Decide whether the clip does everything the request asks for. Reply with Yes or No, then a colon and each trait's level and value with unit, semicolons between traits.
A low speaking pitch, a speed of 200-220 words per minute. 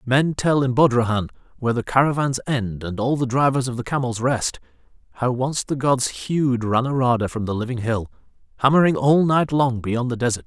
No: low, 125 Hz; average, 190 wpm